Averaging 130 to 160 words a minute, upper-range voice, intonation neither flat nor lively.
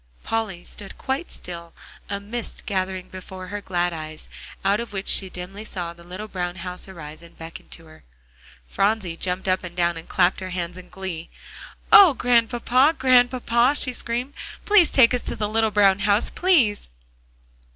No: average, 170 wpm; high, 195 Hz; average, 4.7 semitones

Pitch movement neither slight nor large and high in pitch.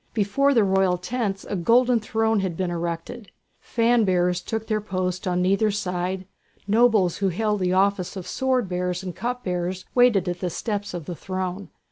Yes: average, 3.5 semitones; high, 195 Hz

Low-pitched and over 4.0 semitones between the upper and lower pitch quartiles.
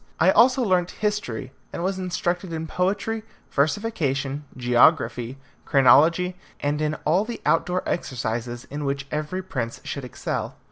No: medium, 155 Hz; wide, 5.4 semitones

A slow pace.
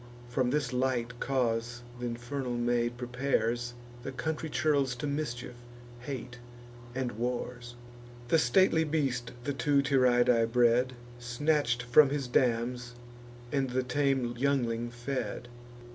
Yes: slow, 120 wpm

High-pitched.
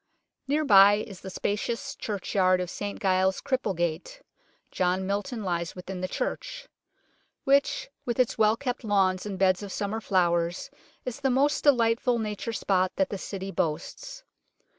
Yes: high, 200 Hz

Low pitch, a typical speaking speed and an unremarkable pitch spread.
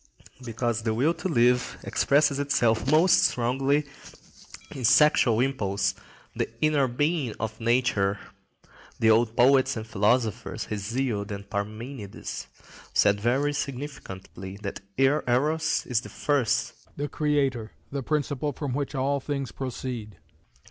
No: low, 125 Hz; slow, 120 wpm; average, 4.3 semitones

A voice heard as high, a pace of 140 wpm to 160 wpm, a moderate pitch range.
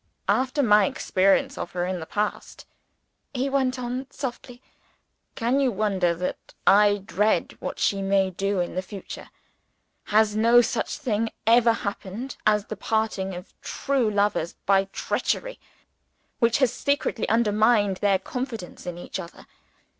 Yes: high, 210 Hz; average, 145 wpm; average, 3.9 semitones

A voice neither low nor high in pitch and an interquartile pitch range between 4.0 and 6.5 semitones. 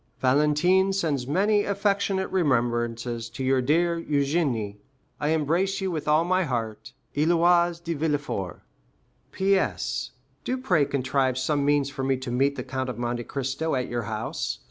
Yes: medium, 145 Hz; average, 5.2 semitones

